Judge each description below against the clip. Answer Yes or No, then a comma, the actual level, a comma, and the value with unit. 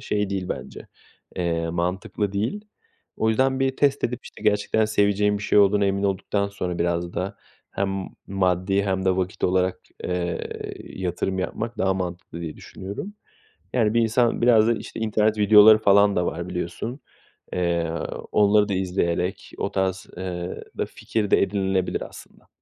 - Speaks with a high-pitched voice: No, low, 100 Hz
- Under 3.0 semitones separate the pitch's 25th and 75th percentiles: Yes, narrow, 2.6 semitones